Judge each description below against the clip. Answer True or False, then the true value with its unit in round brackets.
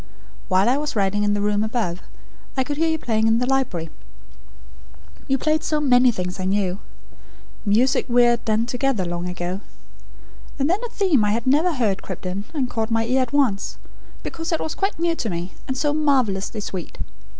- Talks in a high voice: True (235 Hz)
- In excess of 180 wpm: True (195 wpm)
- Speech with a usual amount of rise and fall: False (5.7 semitones)